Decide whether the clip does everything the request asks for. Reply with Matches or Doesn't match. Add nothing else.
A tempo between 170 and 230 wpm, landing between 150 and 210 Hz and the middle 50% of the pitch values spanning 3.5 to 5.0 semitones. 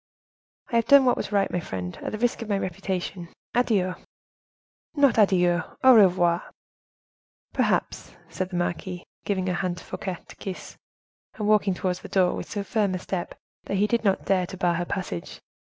Doesn't match